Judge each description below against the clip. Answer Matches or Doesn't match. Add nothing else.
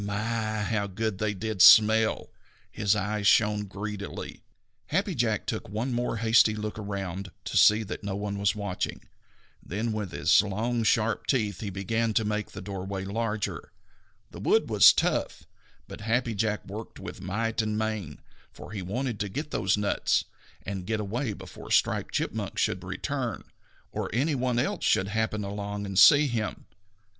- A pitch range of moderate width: Doesn't match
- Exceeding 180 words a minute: Doesn't match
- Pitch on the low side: Matches